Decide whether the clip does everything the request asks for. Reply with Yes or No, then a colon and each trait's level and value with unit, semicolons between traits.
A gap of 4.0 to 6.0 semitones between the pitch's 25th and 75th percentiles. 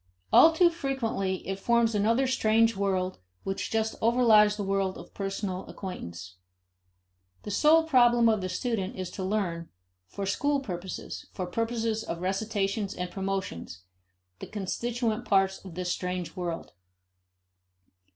No: average, 3.6 semitones